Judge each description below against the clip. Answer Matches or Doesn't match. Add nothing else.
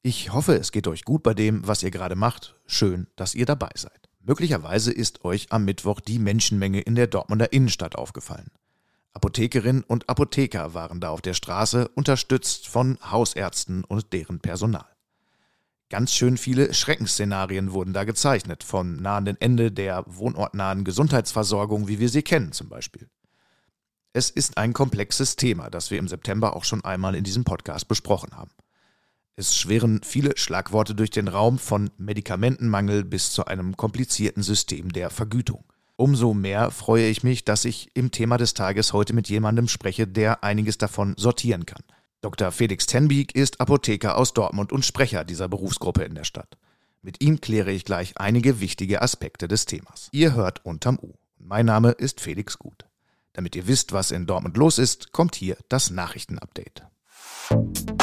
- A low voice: Matches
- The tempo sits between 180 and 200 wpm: Doesn't match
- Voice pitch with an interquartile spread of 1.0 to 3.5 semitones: Doesn't match